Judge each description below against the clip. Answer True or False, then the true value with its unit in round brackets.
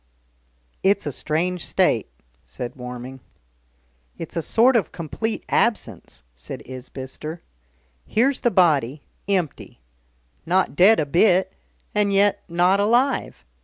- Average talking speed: False (115 wpm)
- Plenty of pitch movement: True (6.9 semitones)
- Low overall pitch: False (175 Hz)